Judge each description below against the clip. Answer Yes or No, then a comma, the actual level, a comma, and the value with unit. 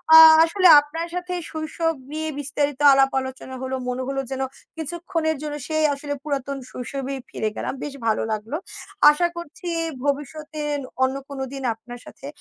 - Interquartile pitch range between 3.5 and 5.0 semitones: No, average, 2.9 semitones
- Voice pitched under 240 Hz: No, very high, 290 Hz